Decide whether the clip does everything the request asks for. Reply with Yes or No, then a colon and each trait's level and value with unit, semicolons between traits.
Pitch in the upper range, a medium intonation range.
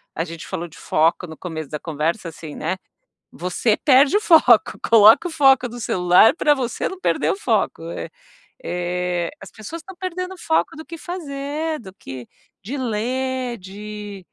No: high, 220 Hz; wide, 8.6 semitones